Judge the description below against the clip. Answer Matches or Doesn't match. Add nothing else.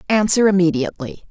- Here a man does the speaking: Doesn't match